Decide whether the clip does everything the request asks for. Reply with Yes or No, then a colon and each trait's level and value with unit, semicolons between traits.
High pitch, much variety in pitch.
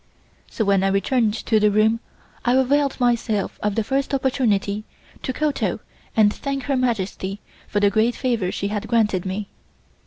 No: high, 220 Hz; average, 3.9 semitones